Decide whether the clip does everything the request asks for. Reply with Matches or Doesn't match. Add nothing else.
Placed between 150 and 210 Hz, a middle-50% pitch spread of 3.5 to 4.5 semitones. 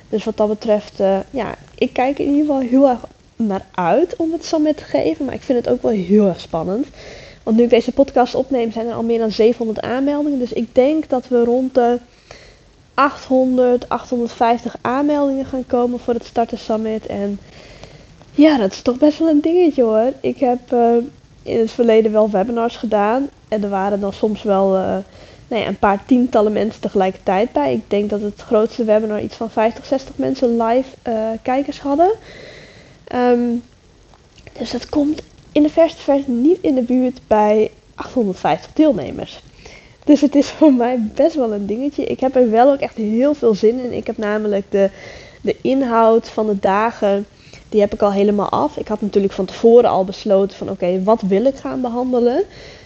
Doesn't match